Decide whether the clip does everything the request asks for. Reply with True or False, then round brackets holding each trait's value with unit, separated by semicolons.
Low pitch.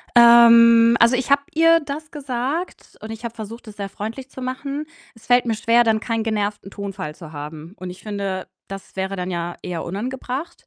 False (225 Hz)